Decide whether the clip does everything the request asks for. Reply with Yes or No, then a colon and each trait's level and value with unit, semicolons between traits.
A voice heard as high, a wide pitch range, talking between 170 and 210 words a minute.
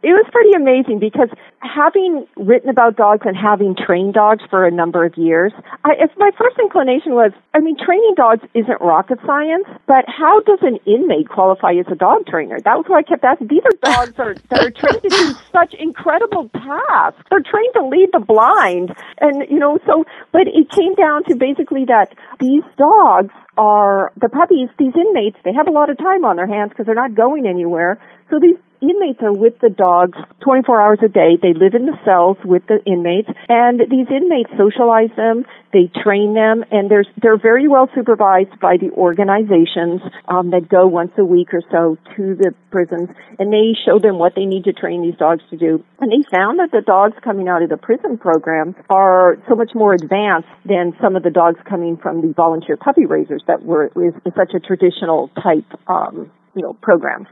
Yes: high, 225 Hz; wide, 8.1 semitones; fast, 205 wpm